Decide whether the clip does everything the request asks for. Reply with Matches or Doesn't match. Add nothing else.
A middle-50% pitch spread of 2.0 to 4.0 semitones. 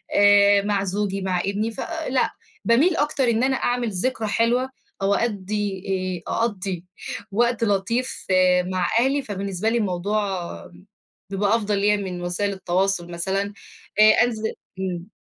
Matches